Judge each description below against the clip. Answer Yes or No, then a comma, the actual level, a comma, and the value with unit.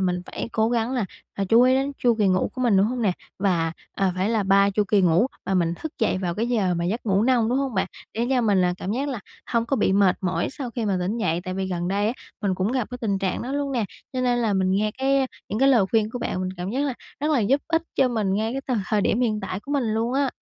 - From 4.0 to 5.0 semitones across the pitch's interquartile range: Yes, average, 4.5 semitones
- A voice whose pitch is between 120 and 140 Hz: No, high, 220 Hz